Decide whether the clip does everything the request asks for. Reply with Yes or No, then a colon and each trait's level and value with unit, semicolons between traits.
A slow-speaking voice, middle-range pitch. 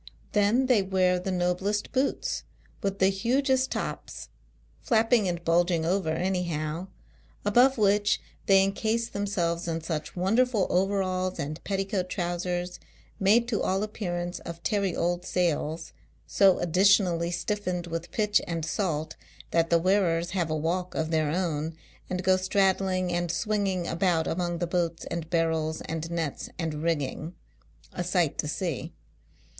No: average, 150 wpm; medium, 180 Hz